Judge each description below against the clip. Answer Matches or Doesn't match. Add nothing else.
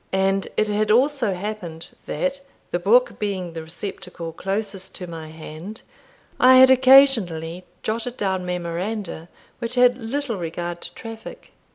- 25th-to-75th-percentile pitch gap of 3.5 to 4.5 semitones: Doesn't match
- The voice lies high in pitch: Matches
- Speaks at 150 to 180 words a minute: Doesn't match